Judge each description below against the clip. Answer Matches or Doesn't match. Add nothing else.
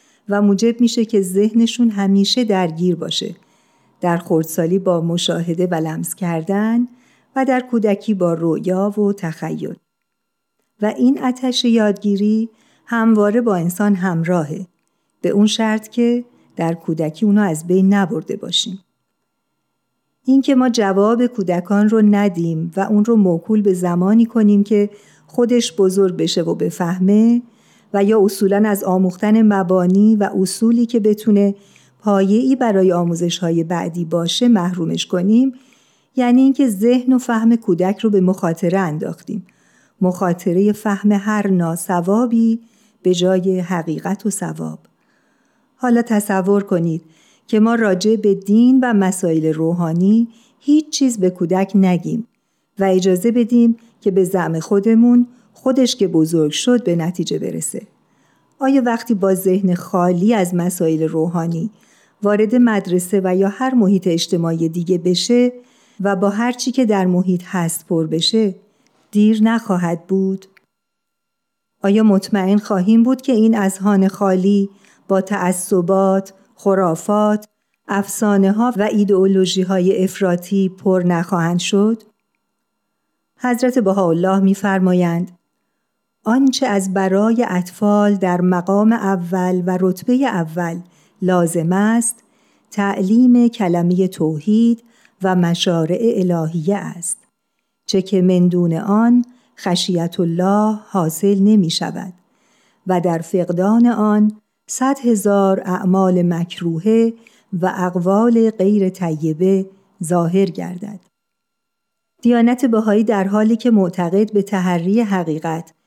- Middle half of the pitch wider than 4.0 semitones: Doesn't match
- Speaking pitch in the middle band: Doesn't match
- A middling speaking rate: Matches